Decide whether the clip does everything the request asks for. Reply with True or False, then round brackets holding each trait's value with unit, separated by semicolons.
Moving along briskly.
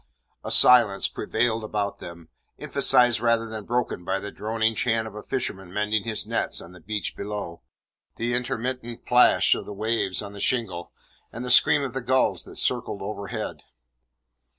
False (170 wpm)